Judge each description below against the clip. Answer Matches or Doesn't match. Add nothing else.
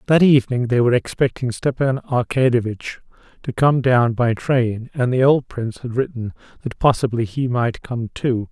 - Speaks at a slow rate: Doesn't match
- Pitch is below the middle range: Matches